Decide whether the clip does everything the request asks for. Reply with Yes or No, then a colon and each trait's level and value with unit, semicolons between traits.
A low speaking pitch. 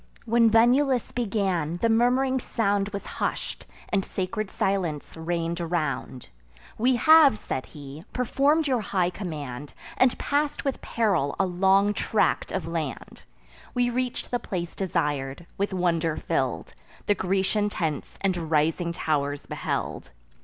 No: high, 190 Hz